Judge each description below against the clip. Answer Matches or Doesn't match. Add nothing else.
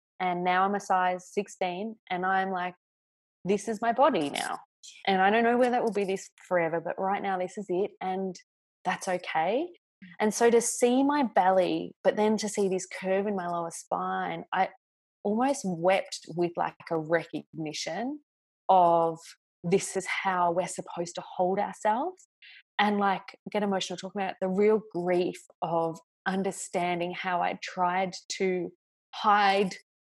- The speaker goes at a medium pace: Matches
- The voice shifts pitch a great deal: Doesn't match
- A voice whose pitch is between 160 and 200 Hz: Matches